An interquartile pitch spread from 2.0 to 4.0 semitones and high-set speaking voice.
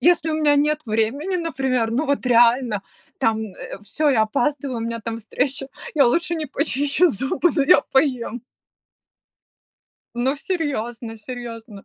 No: average, 4.4 semitones; very high, 260 Hz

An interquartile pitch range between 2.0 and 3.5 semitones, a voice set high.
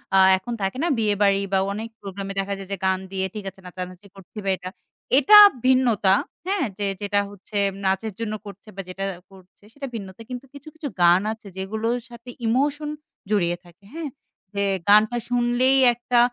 No: average, 4.1 semitones; high, 210 Hz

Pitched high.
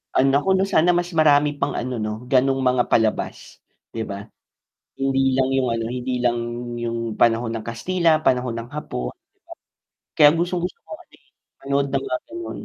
No: low, 135 Hz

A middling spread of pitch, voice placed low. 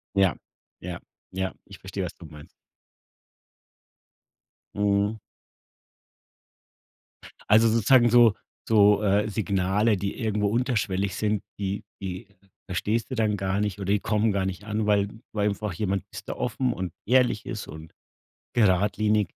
No: narrow, 2.2 semitones; low, 105 Hz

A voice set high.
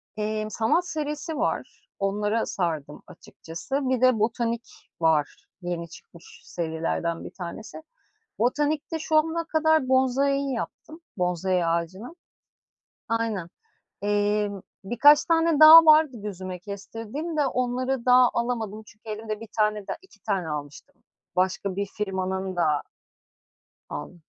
Yes: high, 215 Hz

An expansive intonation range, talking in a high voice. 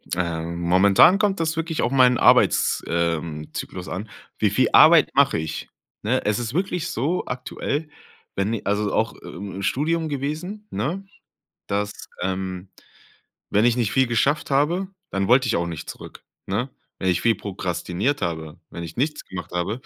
No: wide, 7.8 semitones; low, 110 Hz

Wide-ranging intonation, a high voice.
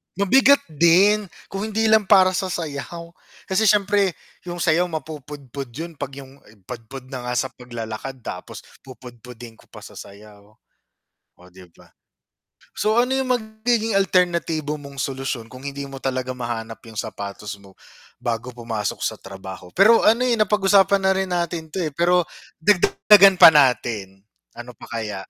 No: wide, 8.1 semitones; medium, 145 Hz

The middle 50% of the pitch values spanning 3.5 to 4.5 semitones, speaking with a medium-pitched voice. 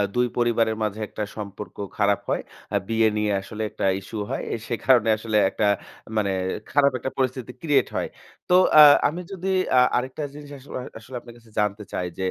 No: average, 3.8 semitones; low, 115 Hz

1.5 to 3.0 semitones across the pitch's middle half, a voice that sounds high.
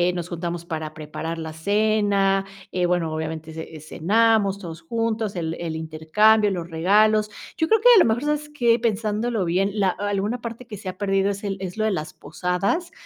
No: average, 4.6 semitones; high, 195 Hz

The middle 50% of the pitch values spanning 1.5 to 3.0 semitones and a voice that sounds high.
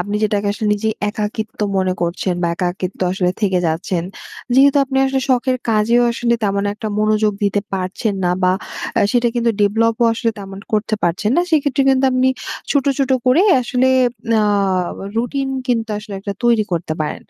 No: average, 3.9 semitones; high, 215 Hz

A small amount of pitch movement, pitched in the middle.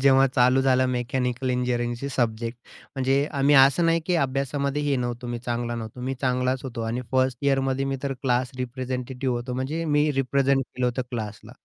No: narrow, 1.8 semitones; low, 130 Hz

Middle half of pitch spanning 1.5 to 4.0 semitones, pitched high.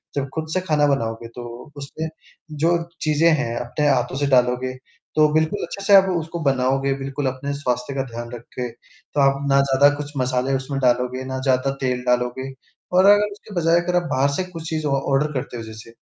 No: average, 3.4 semitones; low, 135 Hz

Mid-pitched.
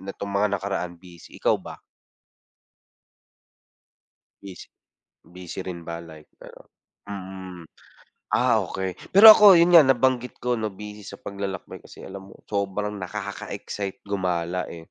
No: low, 100 Hz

